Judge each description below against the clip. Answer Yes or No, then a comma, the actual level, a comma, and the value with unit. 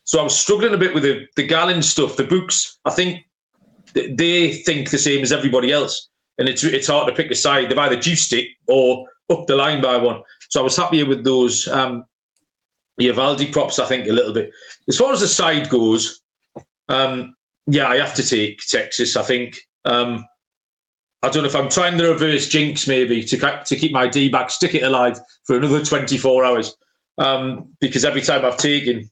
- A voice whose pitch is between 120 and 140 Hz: Yes, low, 135 Hz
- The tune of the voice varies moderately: Yes, average, 3.5 semitones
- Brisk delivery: Yes, fast, 210 wpm